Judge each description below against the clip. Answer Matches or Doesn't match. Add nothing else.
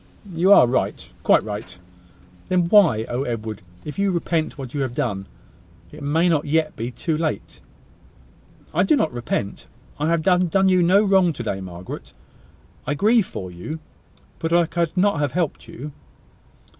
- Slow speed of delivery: Doesn't match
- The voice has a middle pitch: Matches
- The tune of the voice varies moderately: Doesn't match